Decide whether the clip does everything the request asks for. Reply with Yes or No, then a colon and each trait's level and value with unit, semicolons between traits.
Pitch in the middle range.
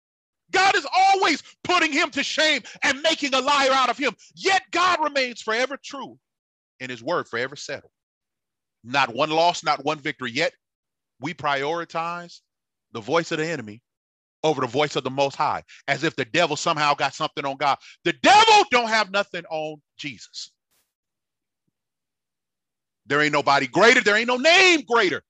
Yes: medium, 175 Hz